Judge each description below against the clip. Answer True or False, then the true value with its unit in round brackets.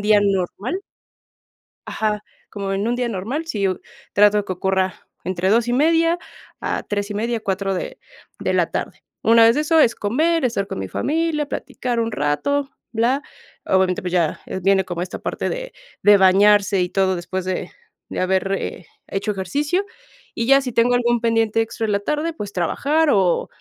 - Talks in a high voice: True (210 Hz)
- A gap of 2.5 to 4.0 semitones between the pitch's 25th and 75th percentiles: False (4.8 semitones)